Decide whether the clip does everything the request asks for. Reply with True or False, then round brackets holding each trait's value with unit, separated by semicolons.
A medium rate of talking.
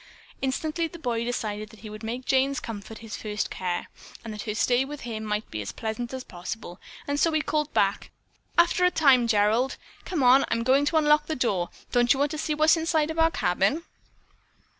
False (215 wpm)